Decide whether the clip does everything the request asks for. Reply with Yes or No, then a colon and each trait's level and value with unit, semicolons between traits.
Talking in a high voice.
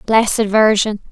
Yes: high, 215 Hz